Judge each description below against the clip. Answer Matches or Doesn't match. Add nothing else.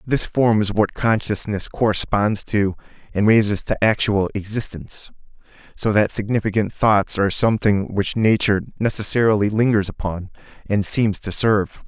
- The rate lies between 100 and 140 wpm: Matches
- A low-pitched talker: Matches